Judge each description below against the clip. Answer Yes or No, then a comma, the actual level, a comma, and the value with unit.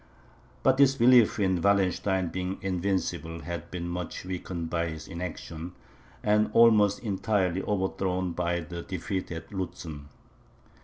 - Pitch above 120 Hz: No, very low, 90 Hz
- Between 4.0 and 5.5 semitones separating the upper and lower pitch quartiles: No, average, 2.7 semitones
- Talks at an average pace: No, slow, 125 wpm